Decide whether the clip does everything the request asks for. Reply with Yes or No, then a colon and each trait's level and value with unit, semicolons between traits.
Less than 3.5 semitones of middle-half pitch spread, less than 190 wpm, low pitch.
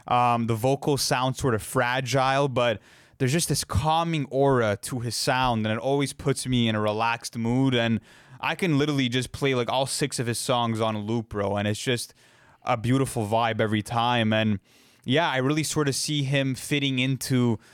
No: average, 2.9 semitones; average, 200 wpm; low, 125 Hz